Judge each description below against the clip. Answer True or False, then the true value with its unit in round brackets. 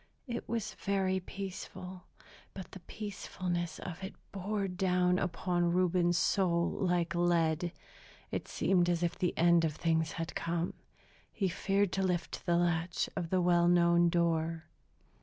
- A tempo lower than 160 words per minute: True (145 wpm)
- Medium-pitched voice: True (175 Hz)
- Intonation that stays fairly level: True (1.7 semitones)